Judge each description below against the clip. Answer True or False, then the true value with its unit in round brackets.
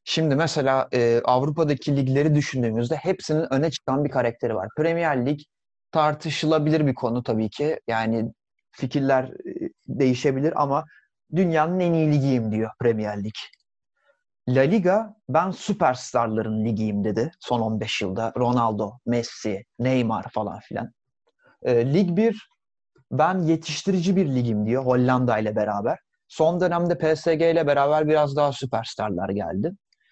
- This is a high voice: False (135 Hz)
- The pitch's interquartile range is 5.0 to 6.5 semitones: True (5.5 semitones)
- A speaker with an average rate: True (130 wpm)